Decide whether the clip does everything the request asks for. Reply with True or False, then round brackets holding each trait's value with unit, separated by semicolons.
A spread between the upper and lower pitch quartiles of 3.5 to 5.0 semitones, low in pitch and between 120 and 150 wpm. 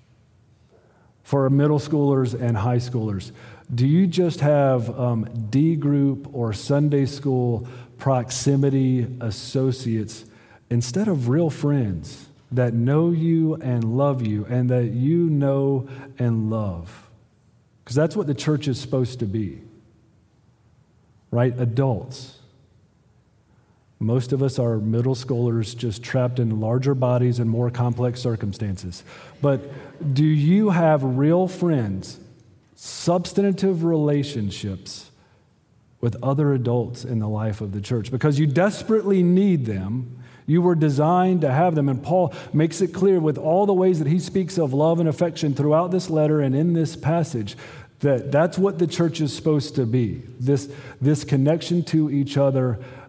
True (4.4 semitones; 130 Hz; 140 wpm)